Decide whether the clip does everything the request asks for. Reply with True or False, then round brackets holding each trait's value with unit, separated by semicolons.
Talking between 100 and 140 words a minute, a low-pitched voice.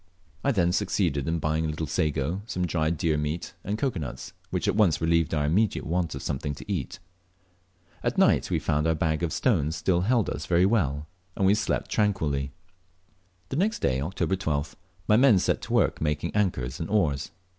False (195 wpm; 80 Hz)